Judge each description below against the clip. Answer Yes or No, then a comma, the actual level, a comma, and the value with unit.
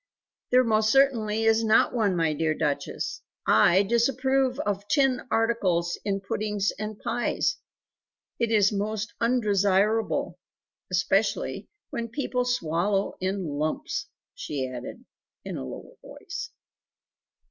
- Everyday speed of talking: No, slow, 115 wpm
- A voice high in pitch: Yes, high, 215 Hz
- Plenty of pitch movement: No, average, 3.8 semitones